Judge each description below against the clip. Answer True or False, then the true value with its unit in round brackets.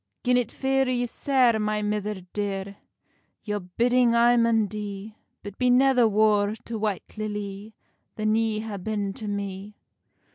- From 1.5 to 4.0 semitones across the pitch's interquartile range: True (2.6 semitones)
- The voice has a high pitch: True (215 Hz)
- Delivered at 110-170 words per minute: True (150 wpm)